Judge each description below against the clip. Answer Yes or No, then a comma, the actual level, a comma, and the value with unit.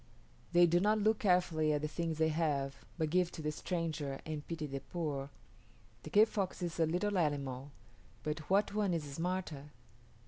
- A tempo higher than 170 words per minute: Yes, average, 180 wpm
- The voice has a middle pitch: Yes, medium, 160 Hz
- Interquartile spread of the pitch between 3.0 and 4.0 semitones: Yes, average, 3.3 semitones